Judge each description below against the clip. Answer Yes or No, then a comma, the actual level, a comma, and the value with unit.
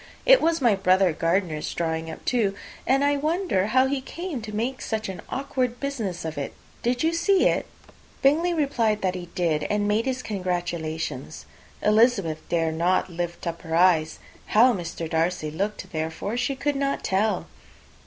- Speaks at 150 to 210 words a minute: Yes, average, 170 wpm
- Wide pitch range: Yes, wide, 7.4 semitones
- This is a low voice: No, high, 205 Hz